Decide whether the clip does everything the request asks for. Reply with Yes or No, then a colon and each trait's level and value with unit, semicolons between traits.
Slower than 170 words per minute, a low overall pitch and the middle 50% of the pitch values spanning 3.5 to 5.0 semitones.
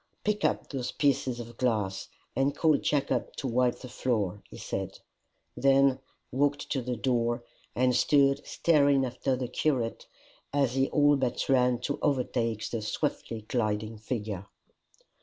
No: average, 145 wpm; low, 125 Hz; average, 2.9 semitones